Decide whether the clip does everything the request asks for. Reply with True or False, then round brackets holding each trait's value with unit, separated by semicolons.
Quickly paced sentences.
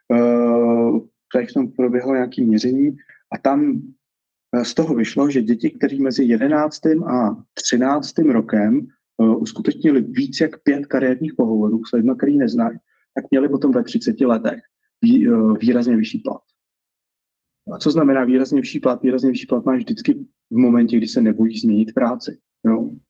False (150 wpm)